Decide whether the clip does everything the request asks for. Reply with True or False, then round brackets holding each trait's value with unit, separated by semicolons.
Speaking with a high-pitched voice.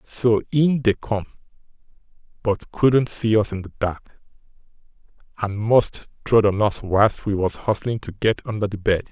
False (110 Hz)